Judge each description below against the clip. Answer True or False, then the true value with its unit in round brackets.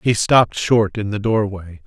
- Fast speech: False (195 wpm)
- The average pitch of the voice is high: False (105 Hz)